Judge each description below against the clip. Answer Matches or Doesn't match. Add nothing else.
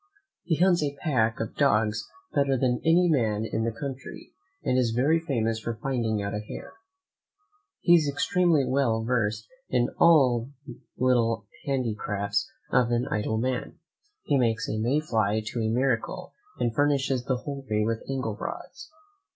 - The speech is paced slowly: Doesn't match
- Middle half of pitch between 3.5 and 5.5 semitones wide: Matches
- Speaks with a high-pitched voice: Doesn't match